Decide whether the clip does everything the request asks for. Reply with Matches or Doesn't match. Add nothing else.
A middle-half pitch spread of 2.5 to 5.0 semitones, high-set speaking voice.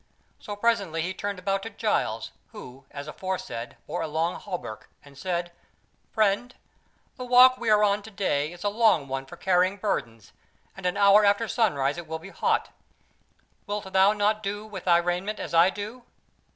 Matches